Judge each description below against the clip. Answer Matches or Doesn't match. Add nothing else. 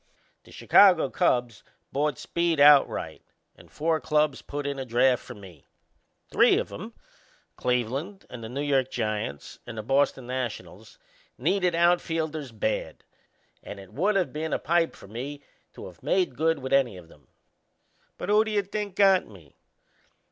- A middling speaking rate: Matches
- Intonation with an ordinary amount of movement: Doesn't match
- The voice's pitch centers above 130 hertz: Matches